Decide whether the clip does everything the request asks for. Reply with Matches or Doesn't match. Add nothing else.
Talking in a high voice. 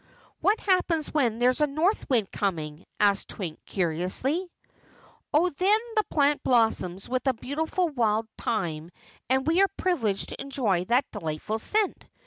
Matches